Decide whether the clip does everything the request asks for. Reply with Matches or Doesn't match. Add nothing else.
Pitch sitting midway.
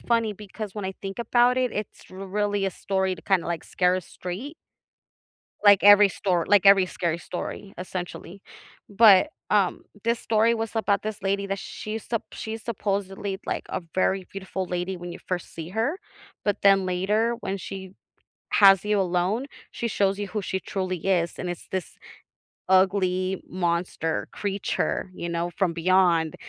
Doesn't match